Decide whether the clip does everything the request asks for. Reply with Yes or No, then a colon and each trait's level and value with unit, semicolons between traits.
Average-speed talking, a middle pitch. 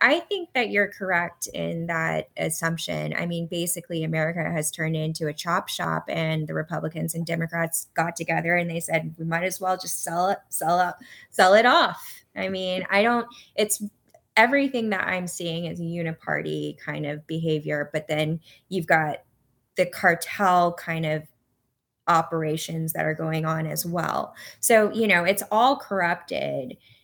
Yes: average, 170 wpm; medium, 165 Hz